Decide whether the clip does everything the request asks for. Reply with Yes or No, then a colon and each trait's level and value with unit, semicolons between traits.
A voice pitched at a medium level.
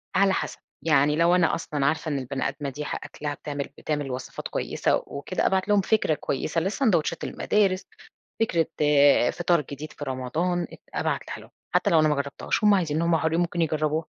Yes: medium, 160 Hz